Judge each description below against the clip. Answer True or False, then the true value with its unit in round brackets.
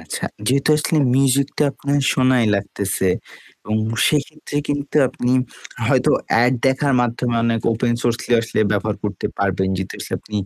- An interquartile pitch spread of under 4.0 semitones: False (4.5 semitones)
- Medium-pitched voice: False (125 Hz)